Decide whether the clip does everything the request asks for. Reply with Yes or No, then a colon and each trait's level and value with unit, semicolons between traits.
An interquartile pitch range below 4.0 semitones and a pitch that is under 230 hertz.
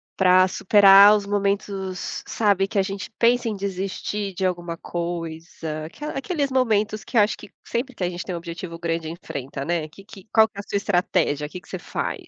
Yes: average, 3.2 semitones; high, 190 Hz